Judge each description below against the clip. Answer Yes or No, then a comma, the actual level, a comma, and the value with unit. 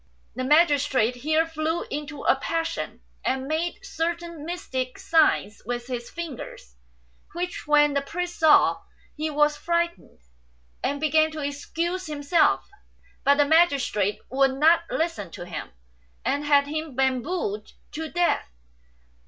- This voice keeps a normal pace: No, slow, 130 wpm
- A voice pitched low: No, very high, 300 Hz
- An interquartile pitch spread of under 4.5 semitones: Yes, average, 3.6 semitones